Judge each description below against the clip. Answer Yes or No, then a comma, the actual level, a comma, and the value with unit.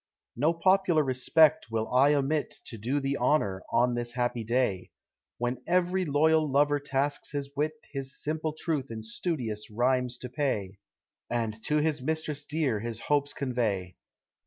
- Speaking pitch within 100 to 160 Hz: Yes, low, 135 Hz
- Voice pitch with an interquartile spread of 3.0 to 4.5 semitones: Yes, average, 4.2 semitones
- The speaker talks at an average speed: Yes, average, 155 wpm